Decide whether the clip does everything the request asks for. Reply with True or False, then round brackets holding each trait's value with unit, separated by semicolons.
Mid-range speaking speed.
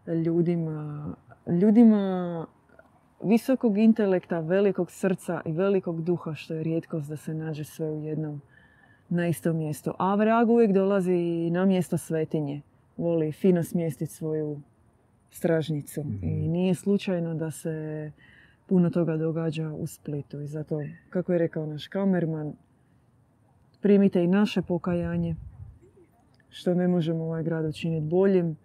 True (130 wpm)